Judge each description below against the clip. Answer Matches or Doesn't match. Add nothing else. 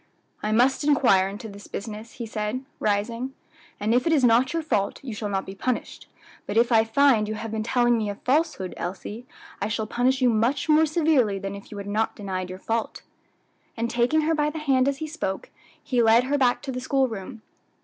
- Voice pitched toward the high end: Matches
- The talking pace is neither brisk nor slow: Doesn't match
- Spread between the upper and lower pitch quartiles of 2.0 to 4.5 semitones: Matches